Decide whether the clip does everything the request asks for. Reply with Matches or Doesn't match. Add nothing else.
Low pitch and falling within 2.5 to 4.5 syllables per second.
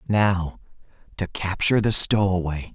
Matches